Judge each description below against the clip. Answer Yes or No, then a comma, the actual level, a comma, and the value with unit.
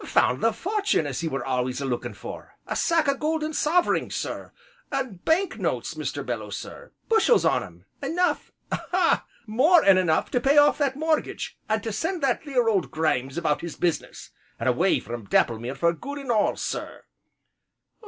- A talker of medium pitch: No, high, 240 Hz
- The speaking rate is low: No, average, 180 wpm